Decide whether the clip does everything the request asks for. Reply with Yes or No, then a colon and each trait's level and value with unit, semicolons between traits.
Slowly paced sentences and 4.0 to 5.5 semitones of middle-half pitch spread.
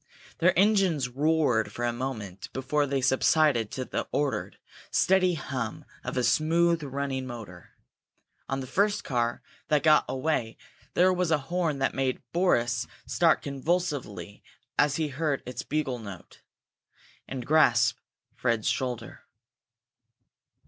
Yes: slow, 130 wpm; average, 4.7 semitones